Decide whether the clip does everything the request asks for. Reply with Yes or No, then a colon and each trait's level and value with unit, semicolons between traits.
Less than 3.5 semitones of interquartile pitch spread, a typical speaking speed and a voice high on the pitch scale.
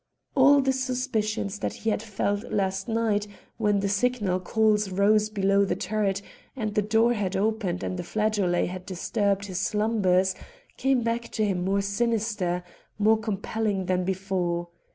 Yes: narrow, 2.5 semitones; average, 155 wpm; high, 205 Hz